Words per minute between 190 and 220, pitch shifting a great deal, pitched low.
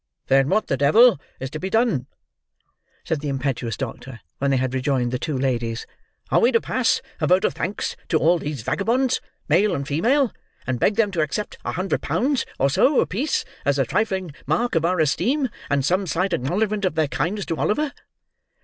No: average, 195 wpm; wide, 7.7 semitones; medium, 165 Hz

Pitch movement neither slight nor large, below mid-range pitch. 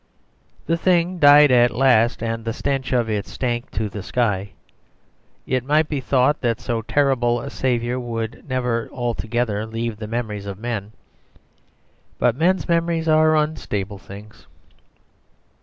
Yes: average, 4.0 semitones; low, 120 Hz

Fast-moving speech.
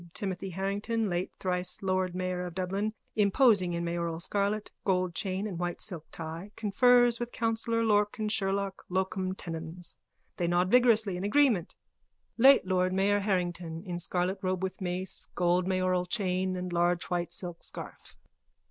No: average, 150 wpm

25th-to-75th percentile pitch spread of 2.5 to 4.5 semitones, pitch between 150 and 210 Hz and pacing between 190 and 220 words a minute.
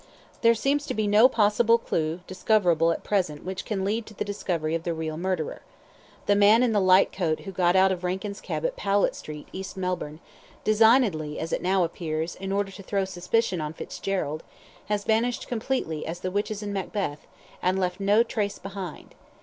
Yes: average, 3.4 semitones; high, 190 Hz; average, 195 wpm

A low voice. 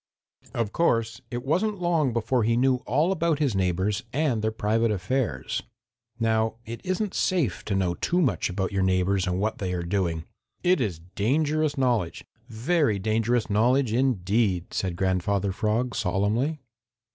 Yes: low, 110 Hz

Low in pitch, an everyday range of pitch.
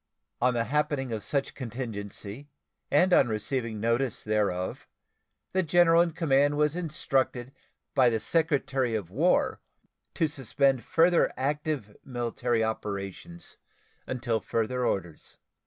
Yes: low, 130 Hz; average, 4.9 semitones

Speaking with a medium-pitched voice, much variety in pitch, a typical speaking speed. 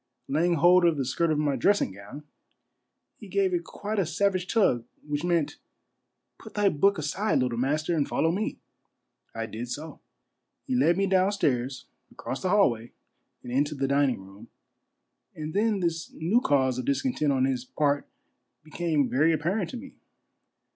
Yes: medium, 155 Hz; wide, 6.1 semitones; average, 170 wpm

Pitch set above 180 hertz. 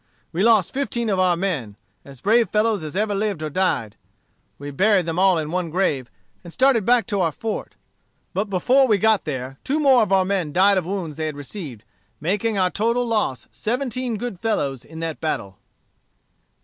Yes: high, 190 Hz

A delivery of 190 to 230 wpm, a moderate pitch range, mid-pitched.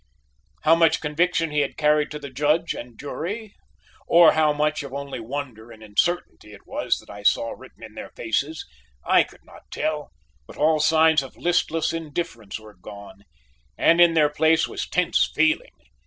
No: average, 175 wpm; average, 4.1 semitones; medium, 150 Hz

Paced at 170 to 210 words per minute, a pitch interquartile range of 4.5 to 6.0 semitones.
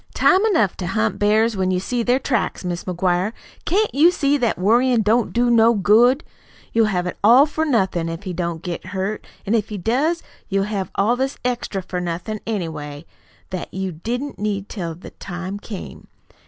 Yes: average, 190 wpm; average, 4.8 semitones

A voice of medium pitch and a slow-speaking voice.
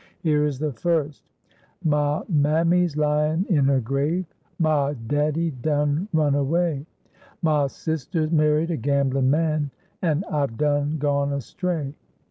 Yes: medium, 150 Hz; slow, 125 wpm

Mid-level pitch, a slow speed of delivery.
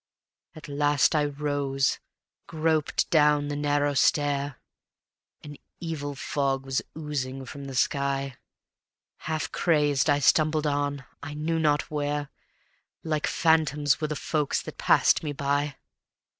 Yes: medium, 145 Hz; slow, 130 wpm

